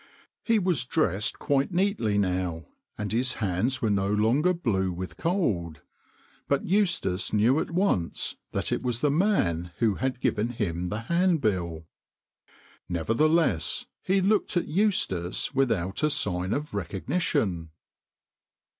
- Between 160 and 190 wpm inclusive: No, slow, 135 wpm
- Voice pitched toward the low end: Yes, low, 115 Hz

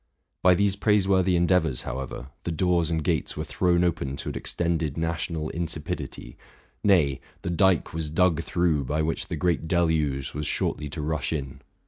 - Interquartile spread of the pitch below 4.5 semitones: Yes, average, 2.9 semitones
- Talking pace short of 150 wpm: No, average, 165 wpm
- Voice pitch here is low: Yes, very low, 80 Hz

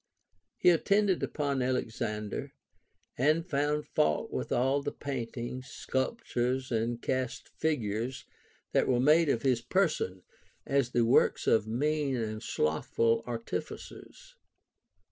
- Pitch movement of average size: Yes, average, 4.2 semitones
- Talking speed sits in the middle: No, slow, 115 wpm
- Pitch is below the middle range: Yes, low, 130 Hz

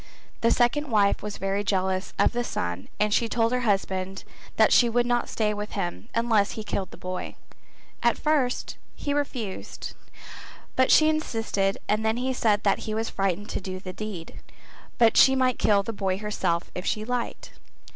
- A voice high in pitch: Yes, high, 215 Hz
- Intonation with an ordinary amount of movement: Yes, average, 3.6 semitones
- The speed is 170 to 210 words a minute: Yes, average, 185 wpm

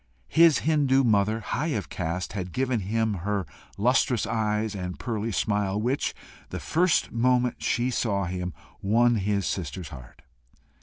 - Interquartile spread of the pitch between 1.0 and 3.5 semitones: No, average, 4.3 semitones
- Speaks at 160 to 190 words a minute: No, average, 145 wpm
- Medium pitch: No, low, 110 Hz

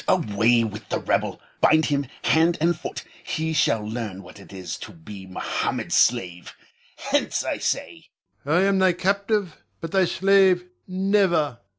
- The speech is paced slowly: No, average, 160 wpm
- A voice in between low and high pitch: Yes, medium, 160 Hz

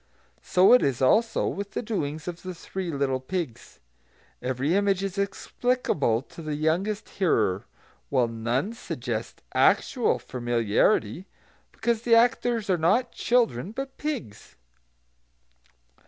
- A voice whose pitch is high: No, medium, 175 Hz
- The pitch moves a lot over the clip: Yes, wide, 8.9 semitones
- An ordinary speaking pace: No, slow, 125 wpm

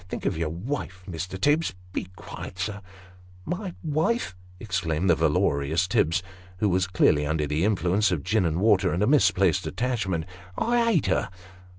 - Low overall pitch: Yes, very low, 95 Hz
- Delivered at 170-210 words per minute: Yes, average, 185 wpm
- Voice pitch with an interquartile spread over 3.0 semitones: Yes, average, 4.1 semitones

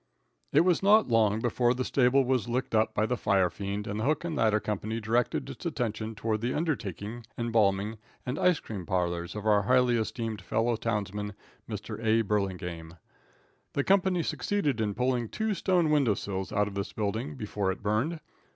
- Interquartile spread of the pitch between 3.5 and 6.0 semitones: Yes, average, 3.9 semitones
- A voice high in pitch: No, low, 110 Hz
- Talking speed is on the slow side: No, average, 180 wpm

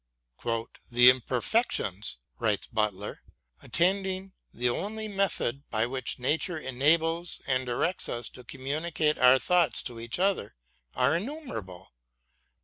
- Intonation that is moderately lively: No, wide, 6.9 semitones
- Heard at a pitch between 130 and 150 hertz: Yes, low, 135 Hz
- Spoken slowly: Yes, slow, 120 wpm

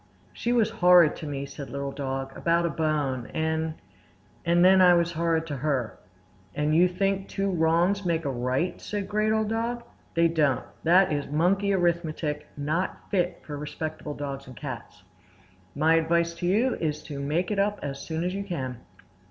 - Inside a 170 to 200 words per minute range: Yes, average, 175 wpm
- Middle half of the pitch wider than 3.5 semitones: Yes, average, 3.9 semitones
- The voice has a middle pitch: Yes, medium, 165 Hz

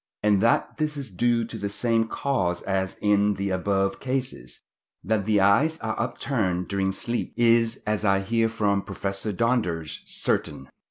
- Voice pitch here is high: No, low, 105 Hz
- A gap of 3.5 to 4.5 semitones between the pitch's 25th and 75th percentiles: No, average, 3.1 semitones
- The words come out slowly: No, average, 160 wpm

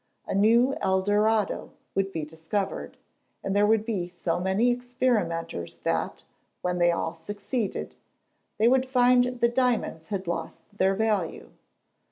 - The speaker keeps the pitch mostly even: No, average, 5.0 semitones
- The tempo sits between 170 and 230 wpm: No, slow, 135 wpm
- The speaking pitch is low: No, high, 205 Hz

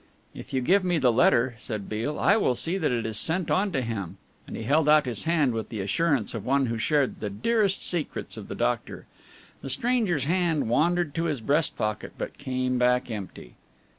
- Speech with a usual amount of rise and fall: No, wide, 6.3 semitones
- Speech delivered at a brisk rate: Yes, fast, 210 wpm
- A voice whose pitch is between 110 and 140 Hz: Yes, low, 135 Hz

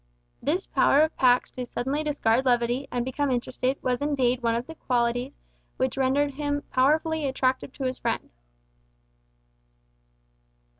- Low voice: No, very high, 260 Hz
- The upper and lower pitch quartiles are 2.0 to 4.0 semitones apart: Yes, average, 2.7 semitones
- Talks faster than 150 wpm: No, average, 140 wpm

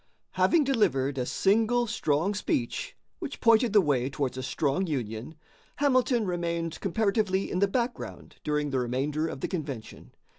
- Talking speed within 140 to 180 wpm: Yes, average, 150 wpm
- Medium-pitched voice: Yes, medium, 170 Hz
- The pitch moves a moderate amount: No, wide, 8.1 semitones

